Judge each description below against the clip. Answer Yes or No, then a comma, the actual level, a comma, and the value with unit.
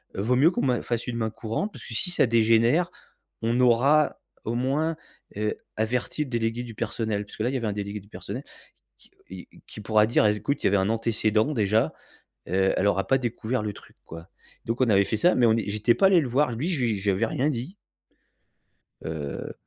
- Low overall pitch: Yes, low, 115 Hz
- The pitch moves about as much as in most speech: Yes, average, 3.3 semitones